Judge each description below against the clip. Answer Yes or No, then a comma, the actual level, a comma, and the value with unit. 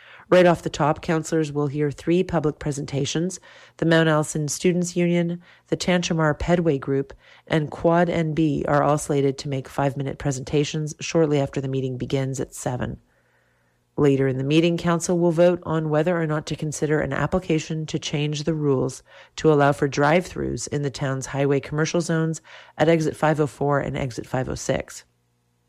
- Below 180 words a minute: Yes, average, 170 wpm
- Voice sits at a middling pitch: Yes, medium, 150 Hz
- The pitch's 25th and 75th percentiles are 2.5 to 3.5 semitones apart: Yes, average, 2.8 semitones